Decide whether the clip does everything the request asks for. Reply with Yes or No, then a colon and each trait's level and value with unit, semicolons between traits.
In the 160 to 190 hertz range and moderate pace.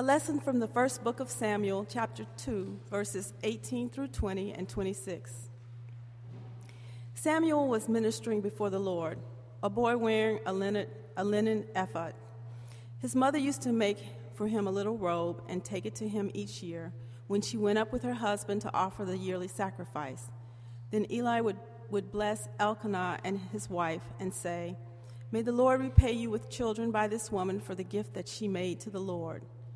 Yes: medium, 185 Hz; average, 180 wpm